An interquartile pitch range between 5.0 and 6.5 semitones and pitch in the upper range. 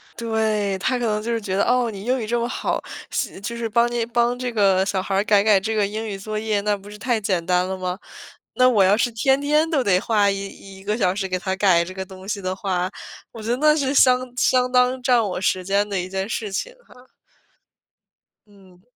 No: average, 3.7 semitones; high, 210 Hz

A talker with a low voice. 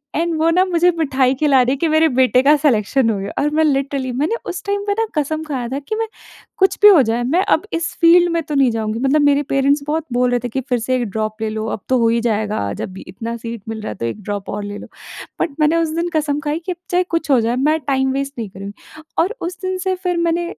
No: very high, 275 Hz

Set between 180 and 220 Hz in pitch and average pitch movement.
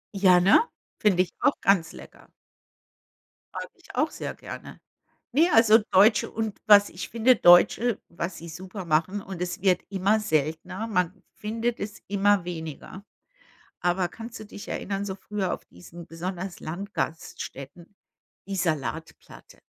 Yes: high, 190 Hz; average, 3.4 semitones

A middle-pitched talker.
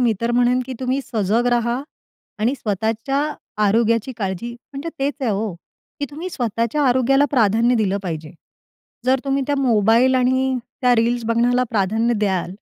No: high, 235 Hz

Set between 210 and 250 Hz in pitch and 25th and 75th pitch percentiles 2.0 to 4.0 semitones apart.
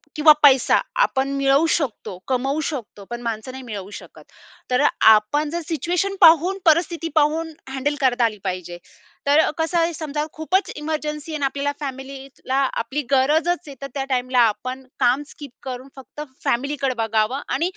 No: very high, 275 Hz; average, 3.5 semitones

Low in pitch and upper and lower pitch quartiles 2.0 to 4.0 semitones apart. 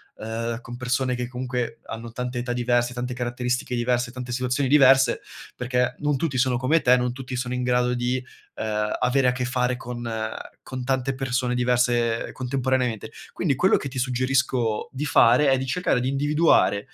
No: low, 125 Hz; narrow, 1.2 semitones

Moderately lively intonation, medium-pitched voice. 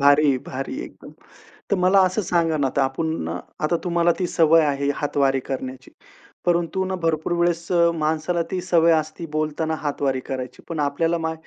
Yes: average, 3.2 semitones; medium, 160 Hz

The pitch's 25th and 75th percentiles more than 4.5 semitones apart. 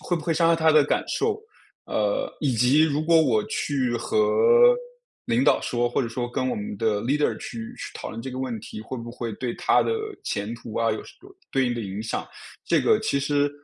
Yes: average, 5.3 semitones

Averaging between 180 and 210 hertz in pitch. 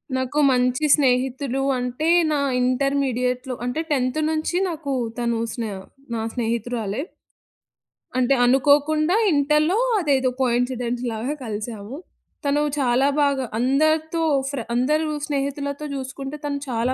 No: very high, 265 Hz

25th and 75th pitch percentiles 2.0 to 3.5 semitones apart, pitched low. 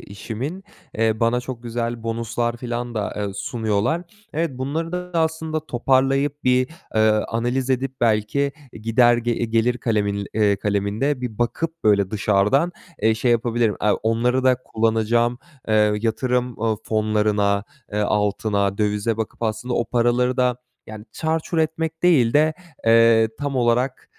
Yes: average, 3.1 semitones; low, 120 Hz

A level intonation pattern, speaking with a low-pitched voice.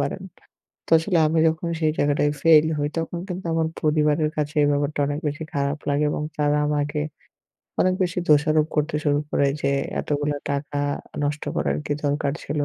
No: narrow, 1.4 semitones; medium, 150 Hz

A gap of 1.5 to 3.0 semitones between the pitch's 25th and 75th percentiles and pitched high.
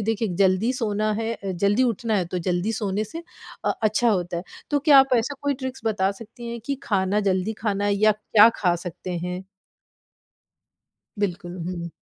No: average, 3.4 semitones; high, 210 Hz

